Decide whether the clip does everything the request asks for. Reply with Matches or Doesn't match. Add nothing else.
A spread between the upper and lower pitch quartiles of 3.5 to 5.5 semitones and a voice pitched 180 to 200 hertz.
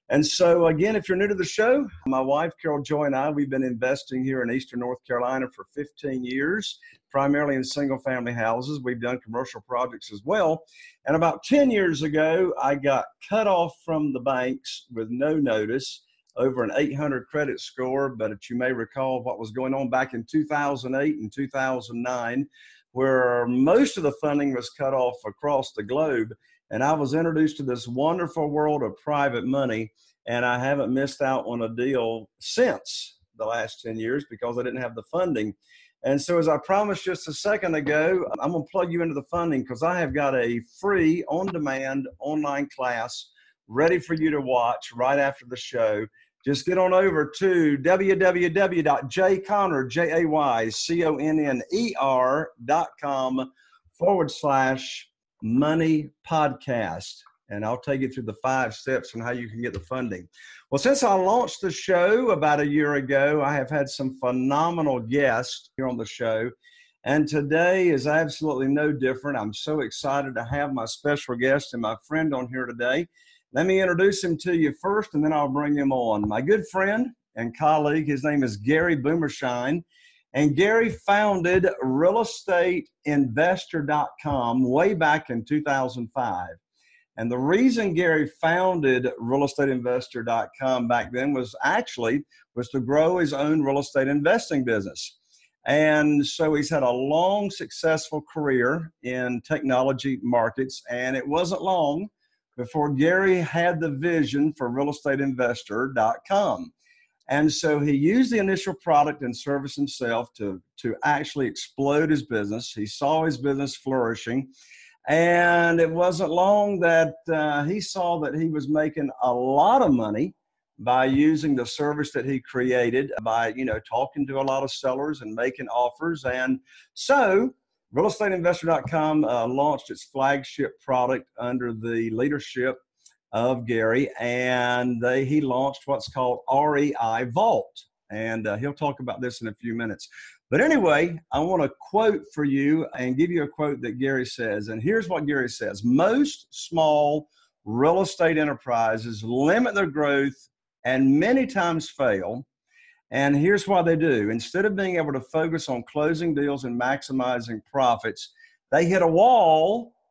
Doesn't match